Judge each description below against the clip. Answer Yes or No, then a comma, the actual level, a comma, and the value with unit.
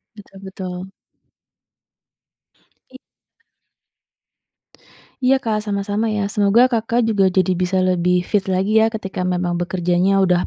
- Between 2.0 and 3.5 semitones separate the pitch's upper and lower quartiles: Yes, average, 2.9 semitones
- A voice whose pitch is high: Yes, high, 195 Hz